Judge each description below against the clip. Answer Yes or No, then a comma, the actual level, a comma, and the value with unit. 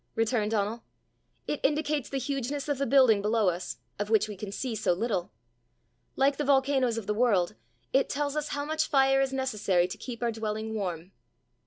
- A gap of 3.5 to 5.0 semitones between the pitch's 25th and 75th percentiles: Yes, average, 4.6 semitones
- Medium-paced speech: Yes, average, 190 wpm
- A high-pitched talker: Yes, high, 235 Hz